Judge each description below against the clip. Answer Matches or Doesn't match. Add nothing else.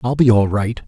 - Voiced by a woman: Doesn't match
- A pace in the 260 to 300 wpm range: Matches